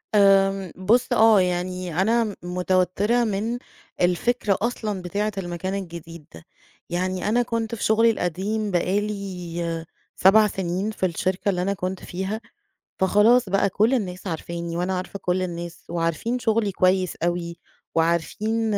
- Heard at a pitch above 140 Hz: Yes, high, 190 Hz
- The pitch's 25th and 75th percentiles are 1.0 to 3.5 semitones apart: Yes, average, 3.2 semitones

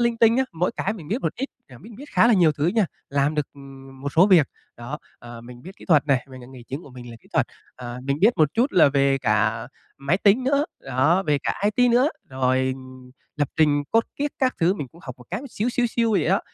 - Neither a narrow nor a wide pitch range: No, wide, 8.4 semitones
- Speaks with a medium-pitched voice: Yes, medium, 150 Hz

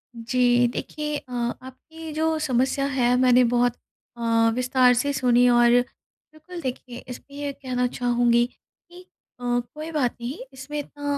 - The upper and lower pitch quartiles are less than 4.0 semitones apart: Yes, average, 2.9 semitones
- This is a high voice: Yes, very high, 255 Hz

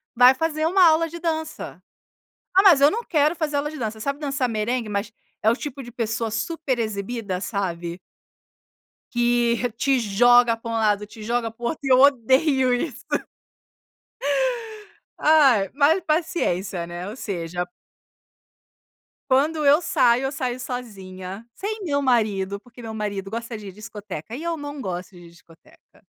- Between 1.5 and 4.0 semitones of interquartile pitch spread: No, wide, 5.5 semitones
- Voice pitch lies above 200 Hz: Yes, high, 240 Hz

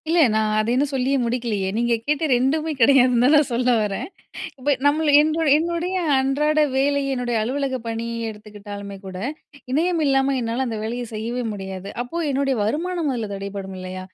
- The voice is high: Yes, very high, 250 Hz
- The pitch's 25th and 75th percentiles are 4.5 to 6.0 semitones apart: Yes, average, 4.9 semitones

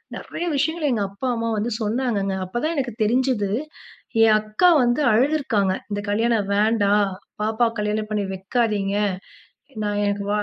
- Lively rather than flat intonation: No, average, 2.9 semitones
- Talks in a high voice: Yes, high, 215 Hz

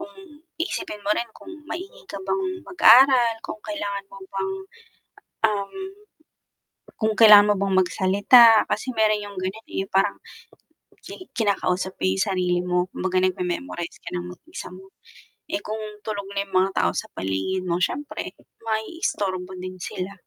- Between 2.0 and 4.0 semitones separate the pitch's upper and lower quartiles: Yes, average, 3.4 semitones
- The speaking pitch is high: Yes, high, 200 Hz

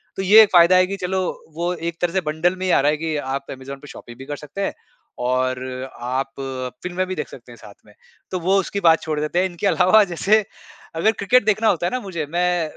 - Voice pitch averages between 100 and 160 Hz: No, medium, 175 Hz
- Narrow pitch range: No, average, 3.9 semitones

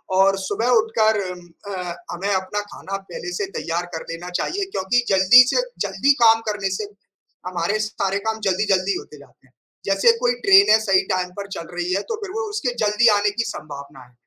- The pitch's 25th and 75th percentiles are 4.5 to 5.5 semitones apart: No, average, 3.7 semitones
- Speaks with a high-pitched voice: Yes, high, 195 Hz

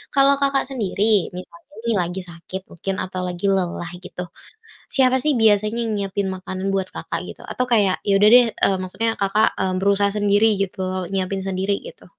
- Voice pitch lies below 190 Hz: No, high, 195 Hz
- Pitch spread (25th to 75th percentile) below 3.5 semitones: Yes, average, 3.1 semitones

